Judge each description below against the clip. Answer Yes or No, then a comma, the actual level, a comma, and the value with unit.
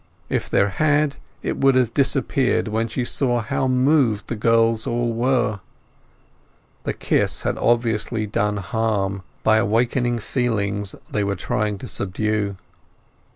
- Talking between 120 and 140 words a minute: Yes, slow, 135 wpm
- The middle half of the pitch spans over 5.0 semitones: No, average, 2.9 semitones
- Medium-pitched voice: No, low, 115 Hz